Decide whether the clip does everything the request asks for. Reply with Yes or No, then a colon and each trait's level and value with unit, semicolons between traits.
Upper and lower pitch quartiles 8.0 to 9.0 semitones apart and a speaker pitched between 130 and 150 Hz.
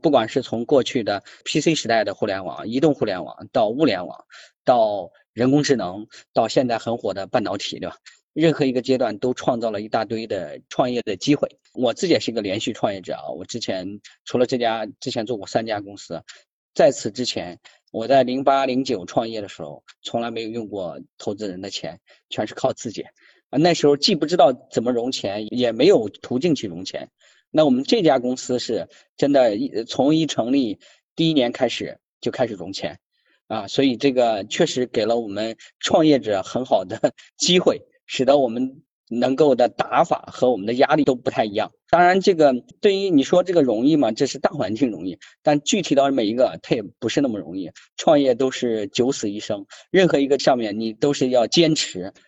No: average, 5.2 semitones; low, 135 Hz